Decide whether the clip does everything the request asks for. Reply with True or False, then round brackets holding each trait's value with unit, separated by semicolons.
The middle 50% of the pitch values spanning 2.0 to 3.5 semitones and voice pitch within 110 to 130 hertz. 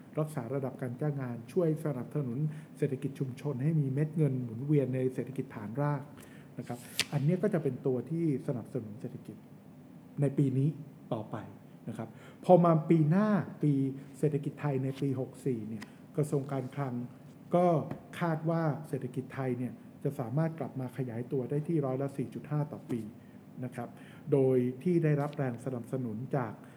False (2.8 semitones; 140 Hz)